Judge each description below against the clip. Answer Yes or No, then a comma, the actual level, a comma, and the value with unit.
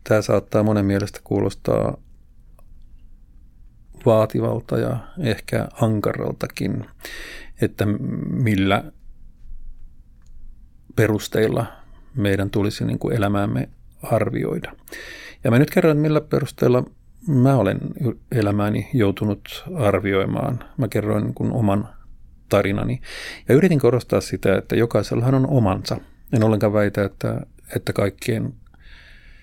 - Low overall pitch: Yes, low, 110 Hz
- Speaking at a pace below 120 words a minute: Yes, average, 100 wpm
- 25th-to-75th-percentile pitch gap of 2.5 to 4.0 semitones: No, average, 4.4 semitones